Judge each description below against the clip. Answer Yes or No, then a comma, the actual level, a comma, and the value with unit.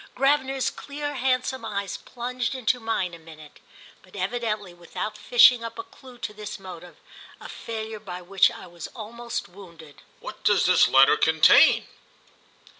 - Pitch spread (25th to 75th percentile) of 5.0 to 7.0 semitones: Yes, average, 5.3 semitones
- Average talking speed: Yes, average, 145 wpm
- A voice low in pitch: No, high, 220 Hz